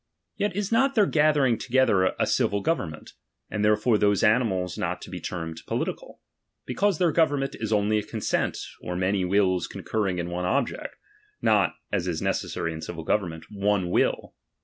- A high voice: No, low, 105 Hz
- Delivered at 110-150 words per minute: No, average, 170 wpm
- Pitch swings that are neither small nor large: No, wide, 6.4 semitones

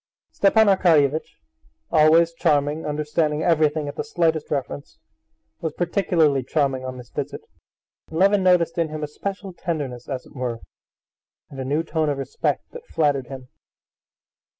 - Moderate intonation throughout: Yes, average, 3.3 semitones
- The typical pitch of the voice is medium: Yes, medium, 155 Hz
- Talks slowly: No, average, 150 wpm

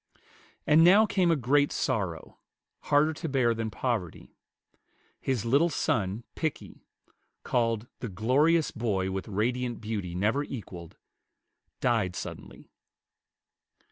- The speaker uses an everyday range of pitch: No, wide, 5.7 semitones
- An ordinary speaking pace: No, slow, 110 wpm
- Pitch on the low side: Yes, low, 120 Hz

